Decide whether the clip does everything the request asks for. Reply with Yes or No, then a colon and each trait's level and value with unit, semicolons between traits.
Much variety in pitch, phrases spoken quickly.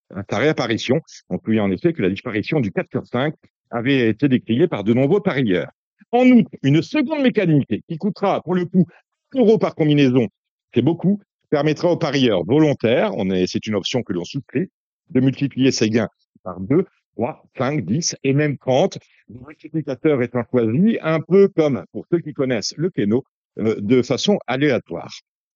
No: wide, 6.5 semitones; average, 180 wpm